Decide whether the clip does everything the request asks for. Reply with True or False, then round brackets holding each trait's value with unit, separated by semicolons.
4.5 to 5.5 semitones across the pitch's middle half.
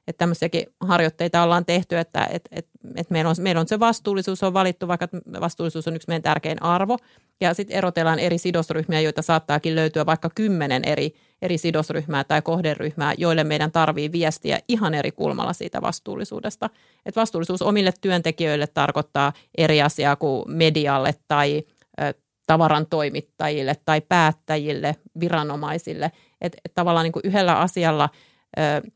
False (2.4 semitones)